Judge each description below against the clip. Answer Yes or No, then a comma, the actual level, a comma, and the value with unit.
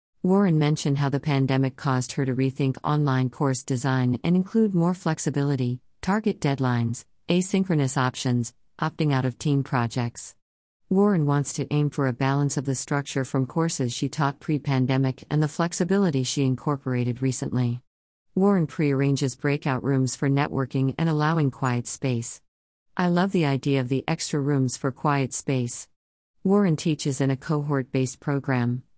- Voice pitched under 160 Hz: Yes, medium, 140 Hz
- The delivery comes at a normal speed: Yes, average, 155 wpm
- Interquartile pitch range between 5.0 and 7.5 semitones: No, average, 2.9 semitones